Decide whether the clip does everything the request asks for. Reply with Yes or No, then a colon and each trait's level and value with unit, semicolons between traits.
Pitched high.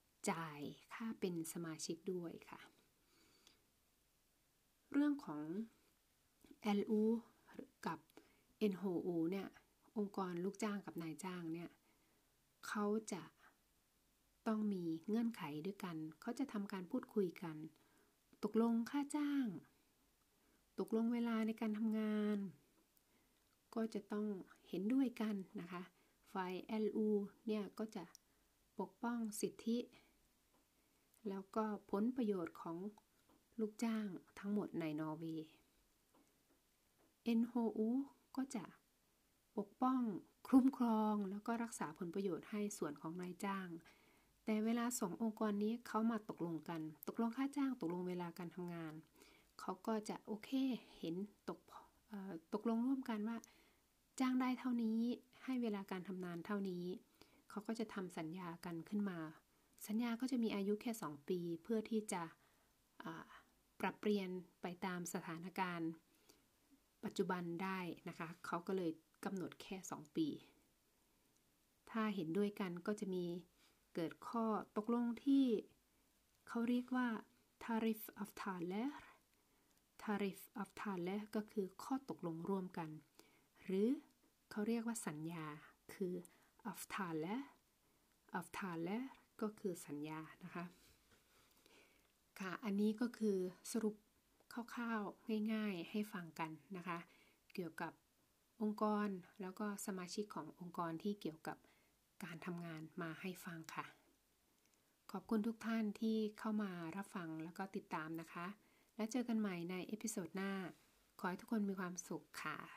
Yes: high, 205 Hz